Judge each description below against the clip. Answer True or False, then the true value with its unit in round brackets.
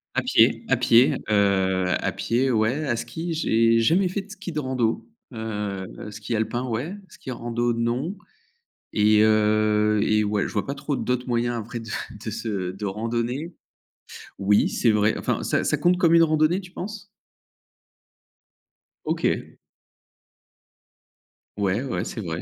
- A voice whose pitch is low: True (115 Hz)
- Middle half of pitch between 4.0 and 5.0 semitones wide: True (4.5 semitones)